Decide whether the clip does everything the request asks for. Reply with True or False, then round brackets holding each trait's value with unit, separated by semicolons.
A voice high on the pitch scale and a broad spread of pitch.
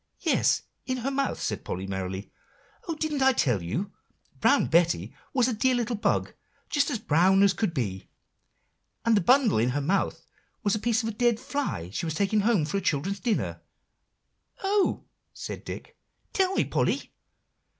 True (205 Hz; 9.0 semitones)